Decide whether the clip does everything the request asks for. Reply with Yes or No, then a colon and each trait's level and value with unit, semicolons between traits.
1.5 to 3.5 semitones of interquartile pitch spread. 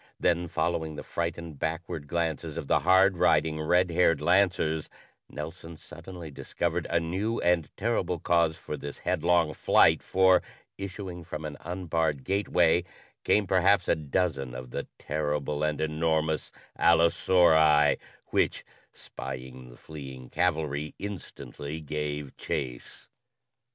Yes: average, 2.8 semitones